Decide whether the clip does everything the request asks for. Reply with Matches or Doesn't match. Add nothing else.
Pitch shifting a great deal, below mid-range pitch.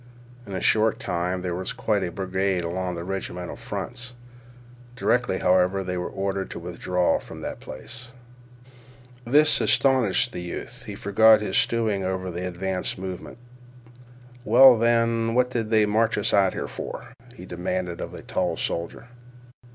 Doesn't match